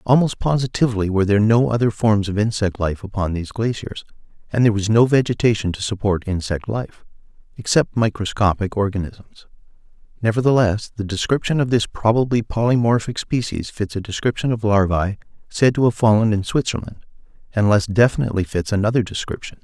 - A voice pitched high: No, low, 105 Hz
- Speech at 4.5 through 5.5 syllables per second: No, 5.8 syllables/s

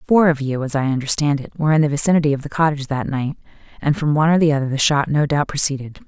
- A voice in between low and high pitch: Yes, medium, 145 Hz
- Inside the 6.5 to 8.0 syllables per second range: Yes, 7.2 syllables/s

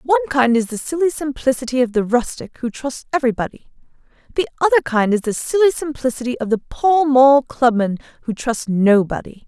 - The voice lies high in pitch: Yes, very high, 260 Hz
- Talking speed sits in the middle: Yes, average, 170 wpm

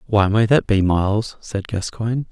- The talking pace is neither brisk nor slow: Yes, average, 180 wpm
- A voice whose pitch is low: Yes, low, 105 Hz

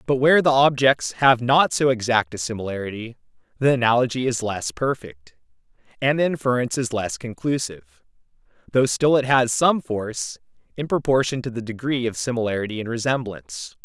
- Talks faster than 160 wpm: No, average, 155 wpm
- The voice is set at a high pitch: No, low, 120 Hz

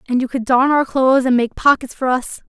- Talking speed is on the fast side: Yes, fast, 265 wpm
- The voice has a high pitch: Yes, very high, 260 Hz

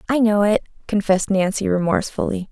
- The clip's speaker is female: Yes, female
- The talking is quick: No, average, 145 wpm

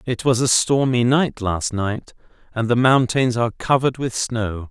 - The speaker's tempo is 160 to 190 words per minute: Yes, average, 180 wpm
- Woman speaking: No, male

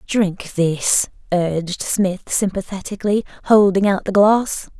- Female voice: Yes, female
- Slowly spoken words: Yes, slow, 125 wpm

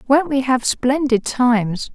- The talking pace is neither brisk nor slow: Yes, average, 155 wpm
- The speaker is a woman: Yes, female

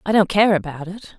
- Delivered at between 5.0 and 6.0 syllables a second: Yes, 5.5 syllables/s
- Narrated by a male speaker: No, female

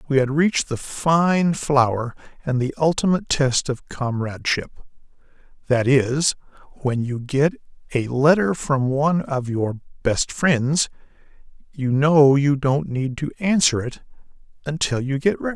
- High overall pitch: No, medium, 140 Hz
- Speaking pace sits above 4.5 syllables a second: No, 4.4 syllables/s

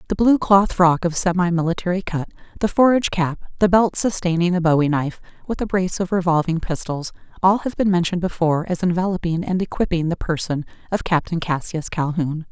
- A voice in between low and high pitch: Yes, medium, 175 Hz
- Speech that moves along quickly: No, average, 170 wpm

